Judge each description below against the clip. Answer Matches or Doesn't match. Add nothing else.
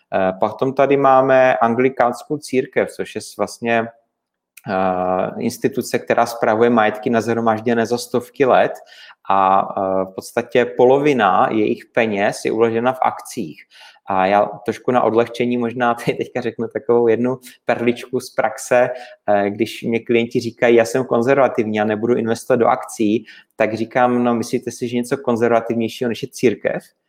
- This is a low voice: Matches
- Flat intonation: Matches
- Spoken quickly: Doesn't match